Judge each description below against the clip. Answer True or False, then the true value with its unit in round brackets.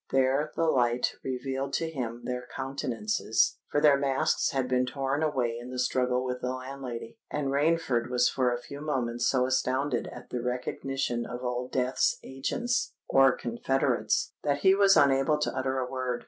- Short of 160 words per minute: False (170 wpm)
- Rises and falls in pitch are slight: True (1.8 semitones)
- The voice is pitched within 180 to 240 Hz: False (130 Hz)